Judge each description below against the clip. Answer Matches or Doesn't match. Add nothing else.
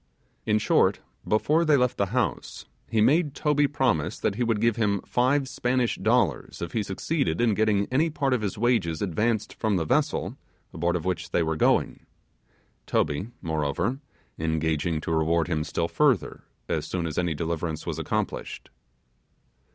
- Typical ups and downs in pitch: Doesn't match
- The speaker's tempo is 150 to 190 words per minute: Matches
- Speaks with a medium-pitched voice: Doesn't match